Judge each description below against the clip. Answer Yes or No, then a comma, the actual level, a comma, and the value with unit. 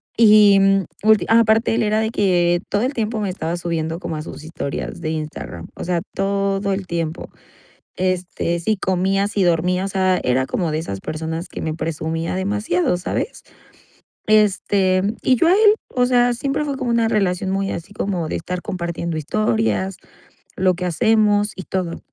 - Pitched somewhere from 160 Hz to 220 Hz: Yes, high, 190 Hz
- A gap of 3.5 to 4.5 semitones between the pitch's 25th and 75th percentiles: Yes, average, 3.9 semitones